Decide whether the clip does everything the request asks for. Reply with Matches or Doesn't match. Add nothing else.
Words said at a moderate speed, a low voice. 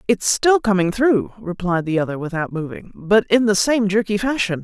Doesn't match